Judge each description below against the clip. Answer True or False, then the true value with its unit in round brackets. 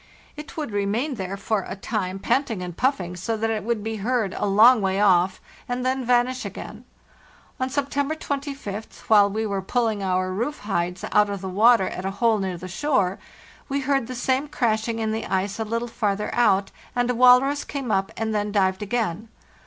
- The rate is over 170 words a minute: True (200 wpm)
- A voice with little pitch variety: False (4.2 semitones)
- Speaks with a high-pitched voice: True (220 Hz)